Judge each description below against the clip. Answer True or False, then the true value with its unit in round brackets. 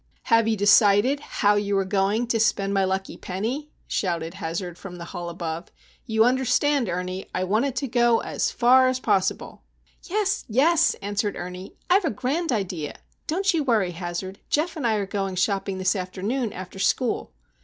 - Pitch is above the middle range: True (205 Hz)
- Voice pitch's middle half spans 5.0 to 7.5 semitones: True (5.3 semitones)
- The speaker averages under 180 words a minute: True (165 wpm)